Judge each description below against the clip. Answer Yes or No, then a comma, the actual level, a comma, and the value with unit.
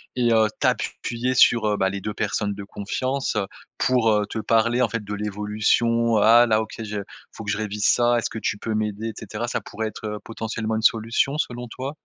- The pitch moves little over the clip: Yes, narrow, 1.9 semitones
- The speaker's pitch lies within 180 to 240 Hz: No, low, 110 Hz